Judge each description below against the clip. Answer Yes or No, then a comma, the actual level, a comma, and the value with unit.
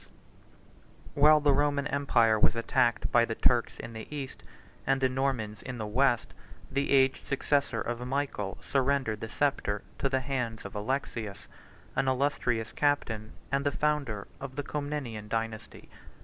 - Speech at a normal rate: Yes, average, 160 wpm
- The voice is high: No, low, 130 Hz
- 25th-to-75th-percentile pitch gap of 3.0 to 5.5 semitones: Yes, average, 3.8 semitones